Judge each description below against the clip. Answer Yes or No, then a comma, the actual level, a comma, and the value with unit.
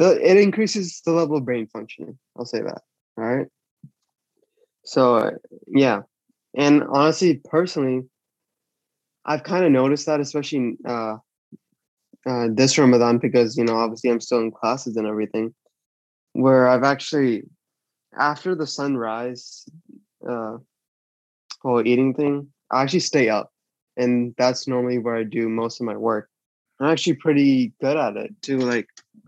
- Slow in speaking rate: No, average, 145 wpm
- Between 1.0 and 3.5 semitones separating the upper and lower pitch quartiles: No, average, 4.1 semitones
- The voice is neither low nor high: No, low, 130 Hz